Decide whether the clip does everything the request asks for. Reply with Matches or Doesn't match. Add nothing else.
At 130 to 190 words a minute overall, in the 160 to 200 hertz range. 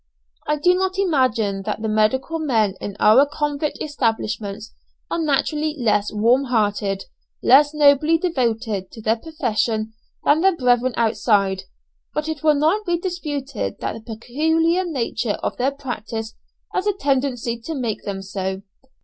Doesn't match